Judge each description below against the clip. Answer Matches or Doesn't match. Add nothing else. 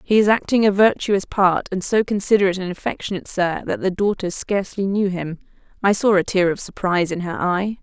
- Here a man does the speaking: Doesn't match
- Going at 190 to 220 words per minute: Matches